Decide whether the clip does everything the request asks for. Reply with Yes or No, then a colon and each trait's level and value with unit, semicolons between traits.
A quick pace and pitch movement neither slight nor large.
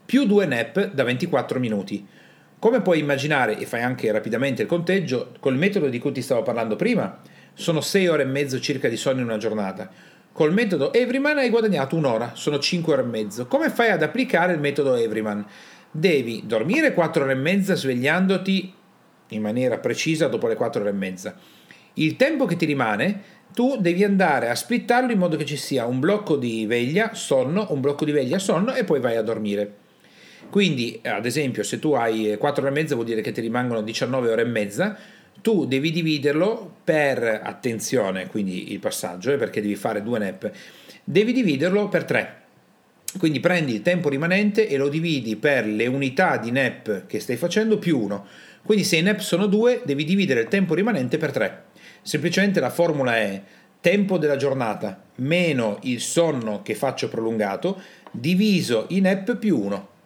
No: fast, 185 wpm; wide, 8.0 semitones